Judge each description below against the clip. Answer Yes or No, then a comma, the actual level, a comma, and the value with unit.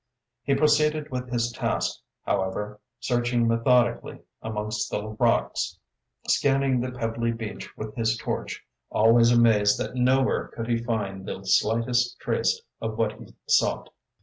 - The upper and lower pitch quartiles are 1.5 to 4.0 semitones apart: Yes, narrow, 2.4 semitones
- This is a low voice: Yes, low, 115 Hz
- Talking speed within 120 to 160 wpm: Yes, slow, 135 wpm